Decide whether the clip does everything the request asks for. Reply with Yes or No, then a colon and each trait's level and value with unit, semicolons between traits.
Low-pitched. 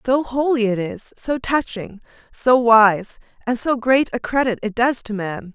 No: high, 235 Hz